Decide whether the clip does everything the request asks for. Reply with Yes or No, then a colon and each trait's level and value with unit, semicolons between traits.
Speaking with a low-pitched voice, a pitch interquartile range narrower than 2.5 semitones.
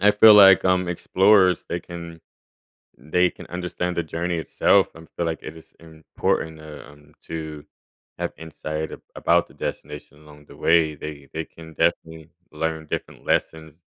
Yes: very low, 80 Hz; narrow, 2.1 semitones